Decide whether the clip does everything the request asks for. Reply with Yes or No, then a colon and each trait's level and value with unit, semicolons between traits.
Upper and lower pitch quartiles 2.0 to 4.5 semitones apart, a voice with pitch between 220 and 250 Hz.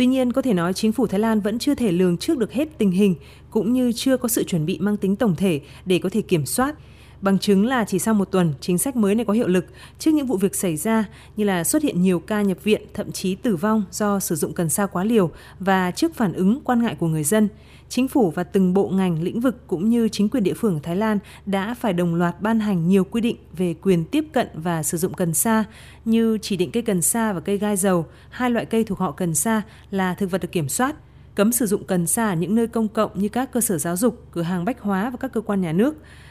No: average, 3.7 semitones; high, 205 Hz